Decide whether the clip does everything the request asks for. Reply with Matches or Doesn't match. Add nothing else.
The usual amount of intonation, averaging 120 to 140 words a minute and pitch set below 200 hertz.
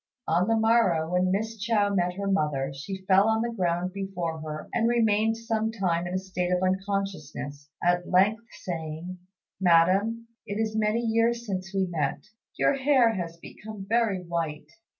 Doesn't match